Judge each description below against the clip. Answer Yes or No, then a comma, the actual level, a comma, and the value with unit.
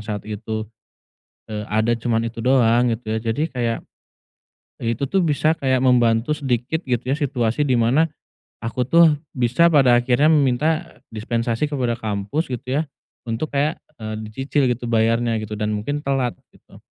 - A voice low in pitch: Yes, low, 120 Hz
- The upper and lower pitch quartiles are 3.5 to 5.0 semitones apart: Yes, average, 3.9 semitones